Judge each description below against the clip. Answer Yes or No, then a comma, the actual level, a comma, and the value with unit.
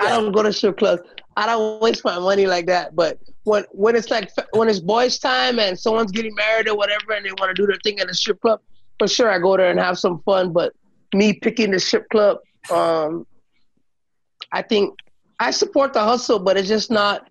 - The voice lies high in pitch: Yes, high, 210 Hz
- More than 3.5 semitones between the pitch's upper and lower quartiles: No, average, 2.8 semitones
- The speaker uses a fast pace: Yes, fast, 225 wpm